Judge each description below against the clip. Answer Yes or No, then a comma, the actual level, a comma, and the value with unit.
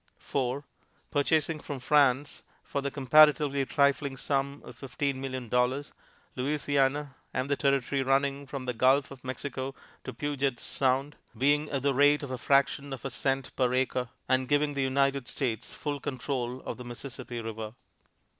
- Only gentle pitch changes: Yes, narrow, 1.8 semitones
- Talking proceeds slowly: No, average, 160 wpm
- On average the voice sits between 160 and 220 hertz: No, low, 135 Hz